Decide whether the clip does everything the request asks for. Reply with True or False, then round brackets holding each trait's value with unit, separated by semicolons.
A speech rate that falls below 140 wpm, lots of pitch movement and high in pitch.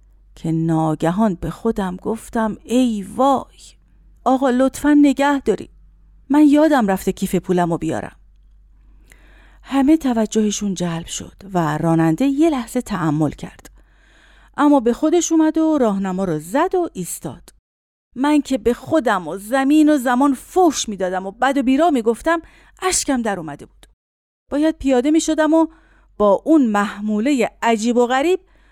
False (145 wpm; 7.2 semitones; 245 Hz)